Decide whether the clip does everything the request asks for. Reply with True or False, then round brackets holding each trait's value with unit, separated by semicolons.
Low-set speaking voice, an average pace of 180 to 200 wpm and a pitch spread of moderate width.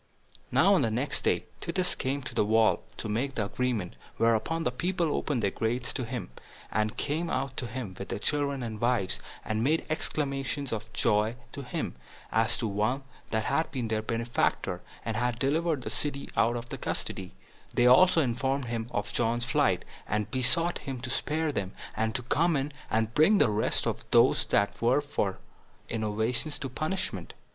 True (125 Hz; 185 wpm; 4.2 semitones)